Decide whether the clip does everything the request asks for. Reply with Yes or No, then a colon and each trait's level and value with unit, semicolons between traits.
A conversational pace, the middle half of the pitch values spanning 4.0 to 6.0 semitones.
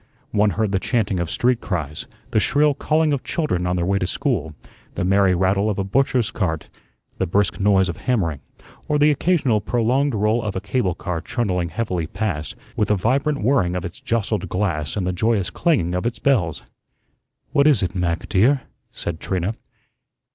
Yes: average, 185 wpm; average, 5.3 semitones